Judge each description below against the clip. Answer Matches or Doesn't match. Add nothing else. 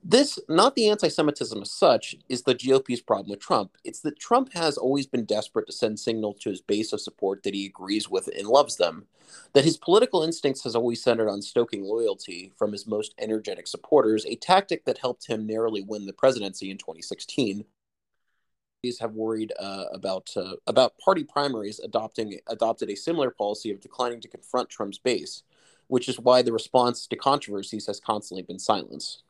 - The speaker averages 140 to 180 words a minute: Doesn't match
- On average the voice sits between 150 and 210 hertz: Doesn't match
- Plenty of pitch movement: Matches